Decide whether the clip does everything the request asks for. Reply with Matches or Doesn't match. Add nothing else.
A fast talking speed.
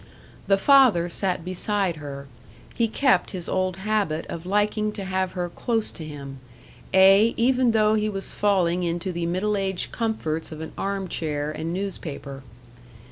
Doesn't match